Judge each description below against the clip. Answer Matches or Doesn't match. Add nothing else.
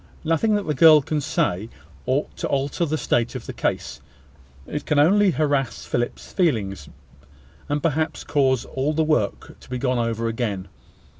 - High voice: Doesn't match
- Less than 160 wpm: Doesn't match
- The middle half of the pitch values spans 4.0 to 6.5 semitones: Matches